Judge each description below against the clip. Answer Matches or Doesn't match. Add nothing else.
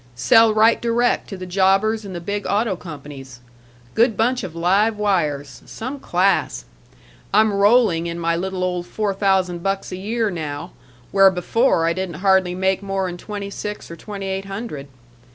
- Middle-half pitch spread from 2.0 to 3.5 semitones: Matches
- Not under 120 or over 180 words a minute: Matches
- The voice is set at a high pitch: Matches